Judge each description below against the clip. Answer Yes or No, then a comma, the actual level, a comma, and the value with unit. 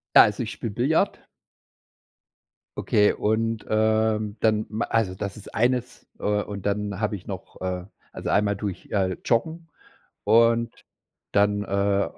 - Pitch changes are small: Yes, narrow, 2.0 semitones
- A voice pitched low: Yes, low, 105 Hz